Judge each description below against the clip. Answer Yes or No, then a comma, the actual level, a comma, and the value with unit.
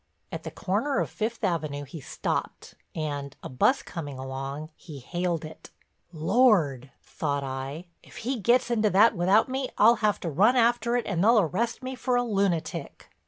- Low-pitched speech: No, medium, 185 Hz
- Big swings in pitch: Yes, wide, 7.9 semitones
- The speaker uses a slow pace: No, average, 175 wpm